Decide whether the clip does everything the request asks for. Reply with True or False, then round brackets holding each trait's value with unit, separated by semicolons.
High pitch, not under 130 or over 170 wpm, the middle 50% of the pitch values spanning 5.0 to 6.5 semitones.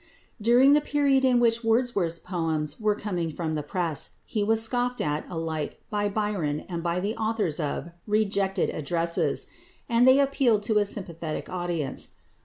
True (200 Hz; 160 wpm; 5.5 semitones)